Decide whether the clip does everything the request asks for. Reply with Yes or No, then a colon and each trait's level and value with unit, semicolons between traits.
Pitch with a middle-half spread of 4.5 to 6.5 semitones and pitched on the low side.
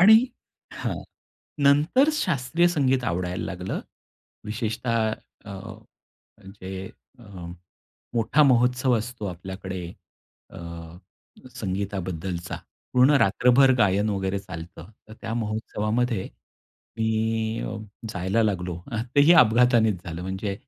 Yes: average, 4.8 semitones; low, 110 Hz